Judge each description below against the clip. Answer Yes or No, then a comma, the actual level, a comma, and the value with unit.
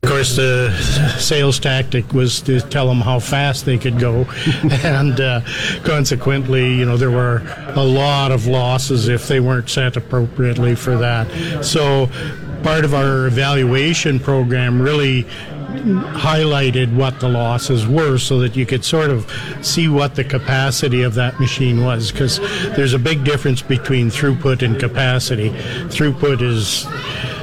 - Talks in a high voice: No, low, 130 Hz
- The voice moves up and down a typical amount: No, narrow, 2.2 semitones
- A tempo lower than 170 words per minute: Yes, average, 150 wpm